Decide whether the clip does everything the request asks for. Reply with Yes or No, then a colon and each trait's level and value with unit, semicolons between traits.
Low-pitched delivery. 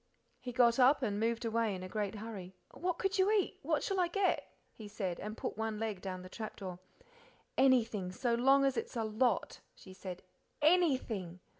No: high, 225 Hz